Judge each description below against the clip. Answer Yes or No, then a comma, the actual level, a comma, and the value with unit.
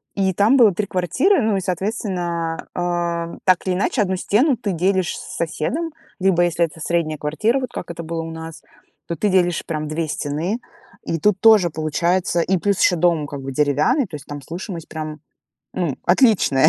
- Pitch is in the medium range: Yes, medium, 175 Hz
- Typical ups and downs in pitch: Yes, average, 3.6 semitones